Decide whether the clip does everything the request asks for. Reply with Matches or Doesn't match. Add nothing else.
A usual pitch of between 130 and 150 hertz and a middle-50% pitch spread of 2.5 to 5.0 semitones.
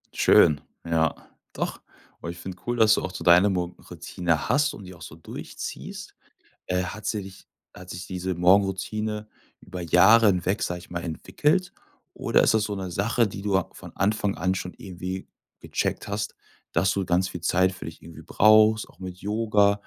Doesn't match